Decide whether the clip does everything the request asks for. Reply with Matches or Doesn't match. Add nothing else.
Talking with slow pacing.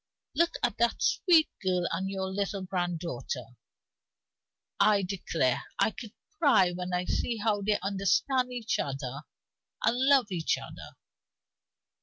Matches